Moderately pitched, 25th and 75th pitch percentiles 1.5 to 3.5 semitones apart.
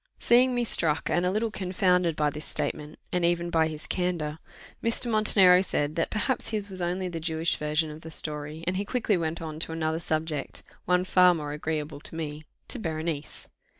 Yes: medium, 165 Hz; average, 3.0 semitones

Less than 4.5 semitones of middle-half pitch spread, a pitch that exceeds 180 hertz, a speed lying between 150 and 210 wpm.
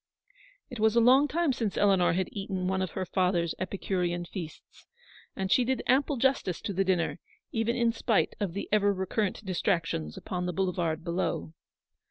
Yes: average, 4.0 semitones; high, 190 Hz; average, 175 wpm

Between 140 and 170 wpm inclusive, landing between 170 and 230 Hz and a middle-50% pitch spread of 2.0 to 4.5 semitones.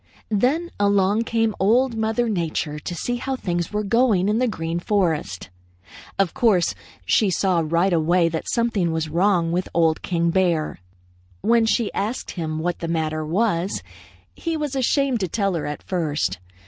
No: average, 165 wpm; high, 190 Hz; average, 5.3 semitones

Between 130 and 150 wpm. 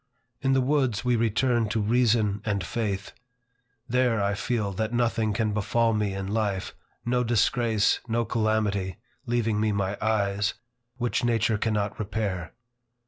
Yes: average, 140 wpm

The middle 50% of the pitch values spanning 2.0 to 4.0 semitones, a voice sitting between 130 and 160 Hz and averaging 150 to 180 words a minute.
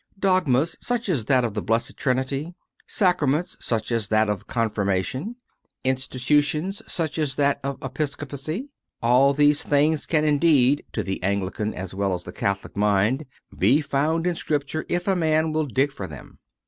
No: wide, 5.6 semitones; medium, 140 Hz; average, 165 wpm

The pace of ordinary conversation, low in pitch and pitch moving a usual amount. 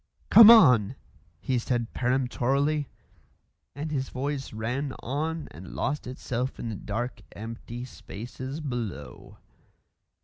No: slow, 110 wpm; low, 125 Hz; average, 3.4 semitones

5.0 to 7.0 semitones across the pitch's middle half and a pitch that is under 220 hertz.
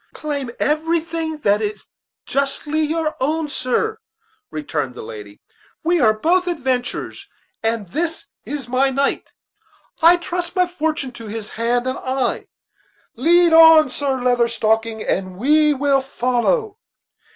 No: wide, 5.4 semitones; very high, 275 Hz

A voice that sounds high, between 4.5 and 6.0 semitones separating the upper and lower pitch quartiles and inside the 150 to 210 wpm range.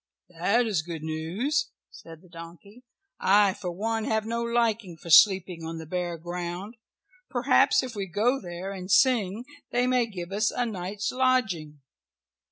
Yes: high, 195 Hz; average, 5.1 semitones; average, 160 wpm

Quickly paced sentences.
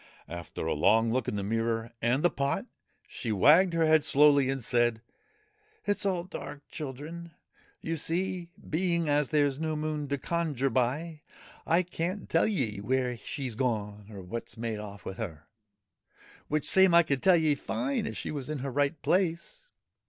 No: average, 185 wpm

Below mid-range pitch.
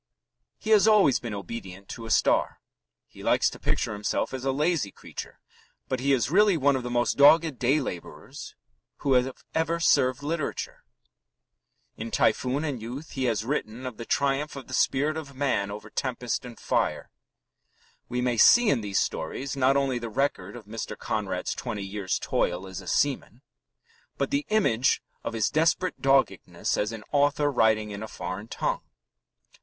Yes: low, 130 Hz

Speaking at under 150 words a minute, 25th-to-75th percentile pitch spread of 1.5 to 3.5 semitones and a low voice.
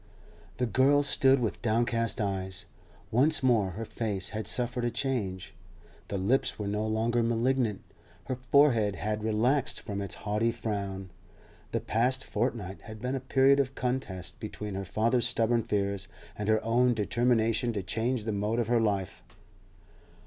No: average, 155 wpm; average, 3.2 semitones; low, 115 Hz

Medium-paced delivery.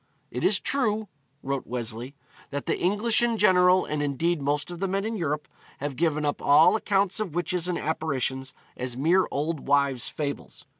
Yes: average, 180 wpm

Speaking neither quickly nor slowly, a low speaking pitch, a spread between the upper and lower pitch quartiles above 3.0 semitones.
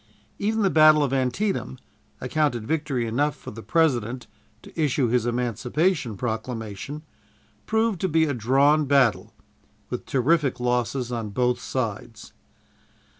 No: slow, 125 wpm; low, 130 Hz; average, 4.4 semitones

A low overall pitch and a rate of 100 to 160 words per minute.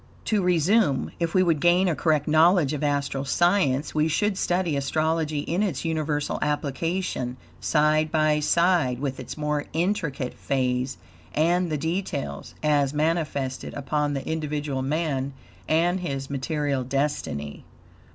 No: medium, 150 Hz; slow, 135 wpm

